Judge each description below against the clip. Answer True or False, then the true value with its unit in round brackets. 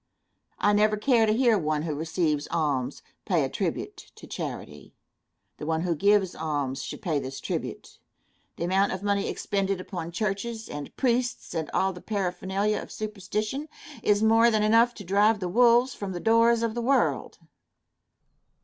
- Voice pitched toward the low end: False (200 Hz)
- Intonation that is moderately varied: True (4.7 semitones)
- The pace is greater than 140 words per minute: True (165 wpm)